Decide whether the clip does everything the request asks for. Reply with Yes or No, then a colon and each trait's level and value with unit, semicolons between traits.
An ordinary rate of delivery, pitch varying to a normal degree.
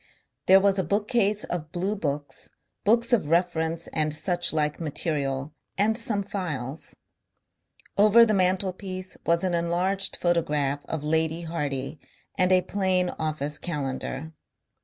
No: slow, 120 wpm; average, 4.2 semitones